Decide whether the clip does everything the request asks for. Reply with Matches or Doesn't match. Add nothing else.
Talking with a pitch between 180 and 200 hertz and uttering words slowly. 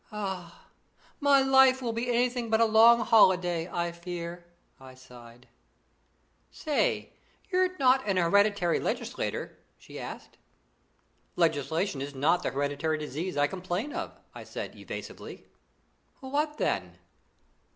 Matches